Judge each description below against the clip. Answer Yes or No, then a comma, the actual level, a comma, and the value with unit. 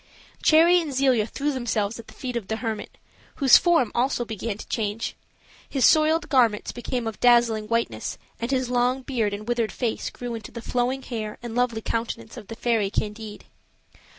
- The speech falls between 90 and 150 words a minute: No, average, 180 wpm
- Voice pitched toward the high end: Yes, high, 235 Hz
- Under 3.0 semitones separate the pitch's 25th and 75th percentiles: Yes, narrow, 2.6 semitones